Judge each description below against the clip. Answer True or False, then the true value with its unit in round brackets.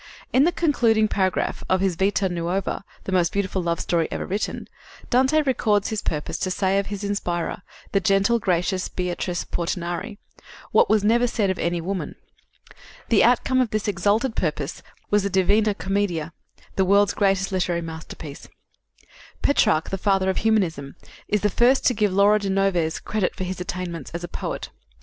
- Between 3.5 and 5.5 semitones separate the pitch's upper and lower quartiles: False (2.9 semitones)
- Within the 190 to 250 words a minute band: False (170 wpm)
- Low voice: False (195 Hz)